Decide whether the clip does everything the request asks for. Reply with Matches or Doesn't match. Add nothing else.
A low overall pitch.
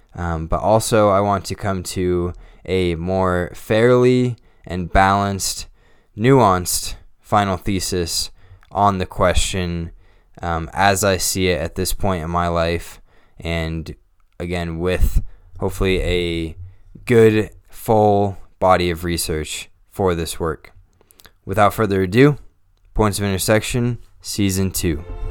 Matches